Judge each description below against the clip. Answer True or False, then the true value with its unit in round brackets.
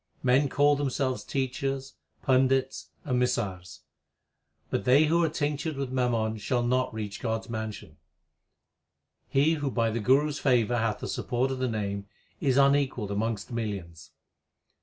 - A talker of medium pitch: False (125 Hz)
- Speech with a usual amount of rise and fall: True (3.6 semitones)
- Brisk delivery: False (155 wpm)